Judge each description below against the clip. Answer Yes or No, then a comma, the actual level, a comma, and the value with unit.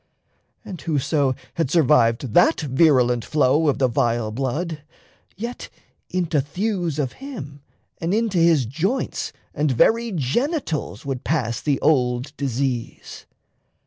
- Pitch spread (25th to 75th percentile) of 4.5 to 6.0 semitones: Yes, average, 4.9 semitones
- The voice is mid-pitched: Yes, medium, 145 Hz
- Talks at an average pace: No, slow, 120 wpm